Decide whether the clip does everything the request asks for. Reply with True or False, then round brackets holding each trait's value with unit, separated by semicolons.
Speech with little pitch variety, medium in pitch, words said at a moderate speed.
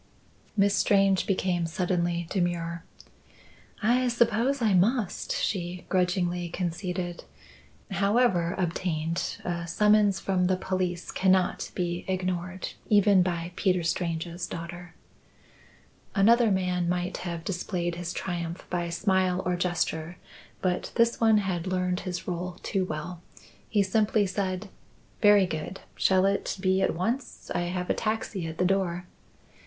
False (2.1 semitones; 180 Hz; 130 wpm)